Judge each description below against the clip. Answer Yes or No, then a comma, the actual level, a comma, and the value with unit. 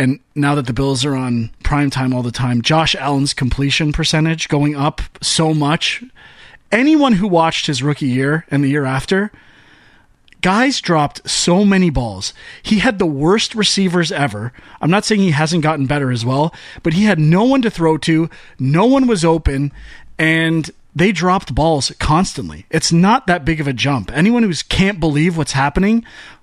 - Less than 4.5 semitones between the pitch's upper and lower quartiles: No, average, 4.8 semitones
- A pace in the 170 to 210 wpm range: Yes, average, 180 wpm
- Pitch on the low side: No, medium, 160 Hz